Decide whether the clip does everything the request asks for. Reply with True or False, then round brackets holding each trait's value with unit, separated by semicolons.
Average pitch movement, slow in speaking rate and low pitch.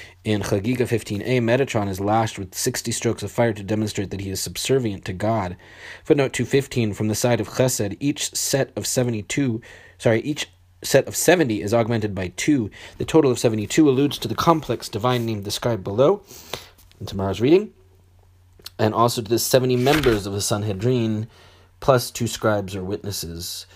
False (3.7 semitones; 170 wpm; 110 Hz)